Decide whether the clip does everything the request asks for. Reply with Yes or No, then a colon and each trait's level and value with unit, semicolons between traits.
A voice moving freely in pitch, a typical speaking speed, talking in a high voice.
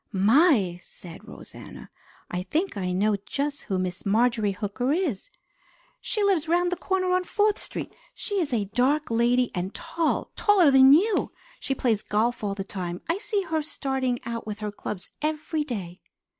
Yes: wide, 8.3 semitones; average, 170 wpm; very high, 250 Hz